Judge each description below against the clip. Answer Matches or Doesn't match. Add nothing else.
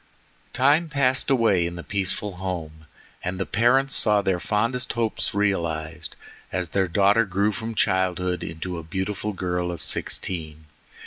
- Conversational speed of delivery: Matches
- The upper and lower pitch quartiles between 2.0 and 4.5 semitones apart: Matches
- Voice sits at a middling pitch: Doesn't match